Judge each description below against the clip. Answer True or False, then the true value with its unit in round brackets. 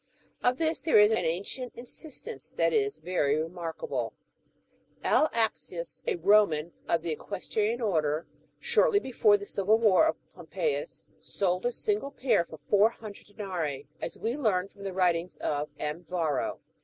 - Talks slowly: False (155 wpm)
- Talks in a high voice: True (205 Hz)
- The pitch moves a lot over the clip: True (6.5 semitones)